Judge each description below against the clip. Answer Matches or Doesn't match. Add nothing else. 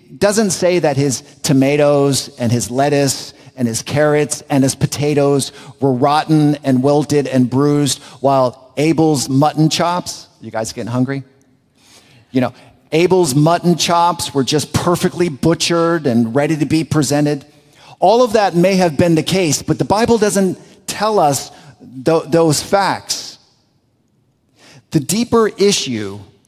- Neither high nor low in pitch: Matches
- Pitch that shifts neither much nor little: Matches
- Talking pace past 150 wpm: Doesn't match